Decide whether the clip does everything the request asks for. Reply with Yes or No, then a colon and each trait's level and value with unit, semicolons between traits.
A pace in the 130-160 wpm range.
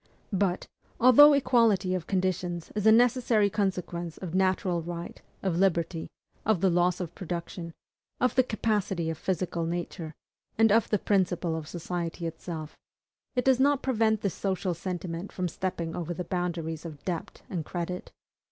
Yes: average, 155 wpm